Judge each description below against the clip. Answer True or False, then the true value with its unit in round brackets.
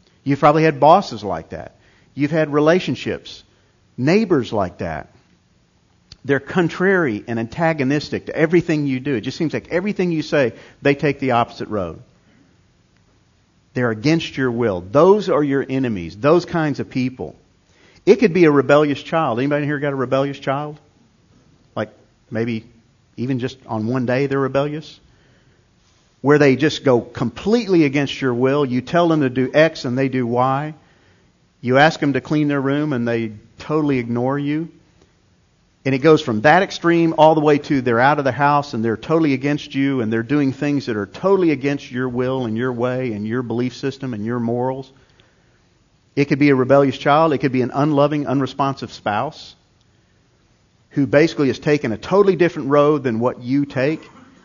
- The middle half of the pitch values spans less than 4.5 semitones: True (3.5 semitones)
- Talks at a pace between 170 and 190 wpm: True (175 wpm)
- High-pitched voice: False (135 Hz)